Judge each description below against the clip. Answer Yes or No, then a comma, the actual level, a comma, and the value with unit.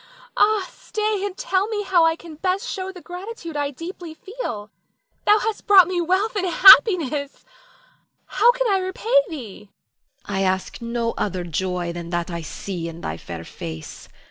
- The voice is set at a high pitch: Yes, very high, 335 Hz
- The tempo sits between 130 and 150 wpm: No, average, 175 wpm